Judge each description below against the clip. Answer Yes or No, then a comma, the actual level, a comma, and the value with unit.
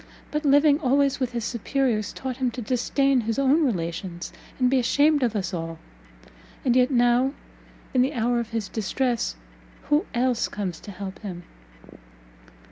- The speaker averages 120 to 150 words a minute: No, average, 160 wpm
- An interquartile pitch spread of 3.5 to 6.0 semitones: Yes, average, 4.2 semitones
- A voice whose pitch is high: Yes, high, 245 Hz